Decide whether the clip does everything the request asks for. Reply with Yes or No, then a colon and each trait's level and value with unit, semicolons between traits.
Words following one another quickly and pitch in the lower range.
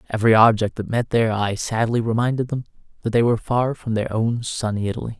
Yes: fast, 210 wpm; low, 115 Hz